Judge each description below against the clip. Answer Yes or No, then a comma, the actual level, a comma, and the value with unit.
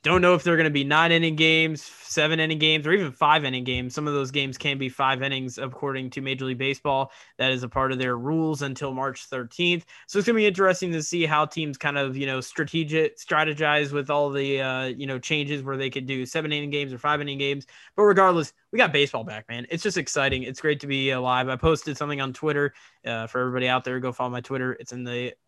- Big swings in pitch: No, average, 3.1 semitones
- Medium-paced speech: No, fast, 250 wpm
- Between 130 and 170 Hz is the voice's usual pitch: Yes, medium, 140 Hz